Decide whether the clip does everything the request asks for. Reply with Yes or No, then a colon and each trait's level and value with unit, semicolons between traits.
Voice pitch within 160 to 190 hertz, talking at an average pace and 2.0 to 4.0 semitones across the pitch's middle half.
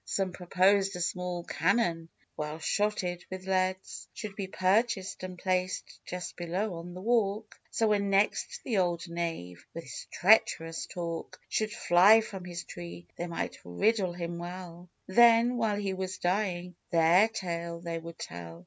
Yes: medium, 185 Hz; average, 155 wpm; average, 2.8 semitones